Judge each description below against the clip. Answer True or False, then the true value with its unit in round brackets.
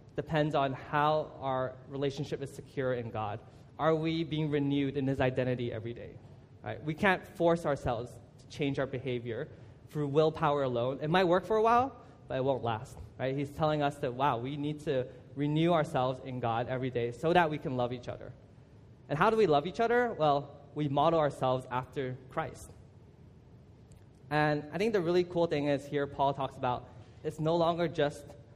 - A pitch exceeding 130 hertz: True (140 Hz)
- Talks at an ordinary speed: True (190 wpm)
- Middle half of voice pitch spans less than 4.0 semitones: True (3.3 semitones)